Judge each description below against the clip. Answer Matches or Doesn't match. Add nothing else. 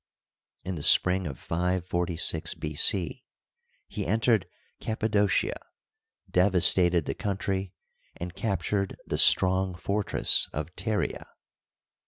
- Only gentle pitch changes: Matches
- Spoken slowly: Matches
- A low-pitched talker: Matches